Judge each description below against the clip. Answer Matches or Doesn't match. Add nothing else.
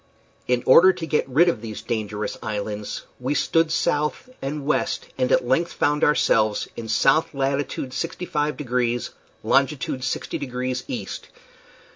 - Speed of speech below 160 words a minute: Matches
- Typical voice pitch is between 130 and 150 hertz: Matches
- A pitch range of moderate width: Matches